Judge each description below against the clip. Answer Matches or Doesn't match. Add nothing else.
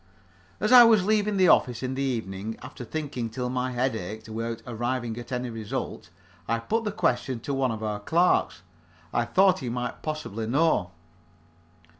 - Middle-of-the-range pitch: Doesn't match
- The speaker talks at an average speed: Matches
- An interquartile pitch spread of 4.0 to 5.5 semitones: Matches